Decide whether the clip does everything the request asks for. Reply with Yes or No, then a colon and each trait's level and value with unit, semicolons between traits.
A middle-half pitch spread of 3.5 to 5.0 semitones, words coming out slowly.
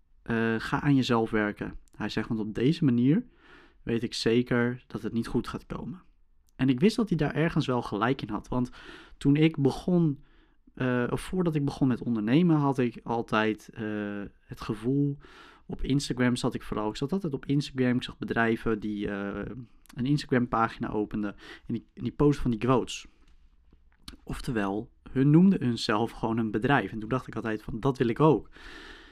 No: average, 4.4 semitones; average, 190 wpm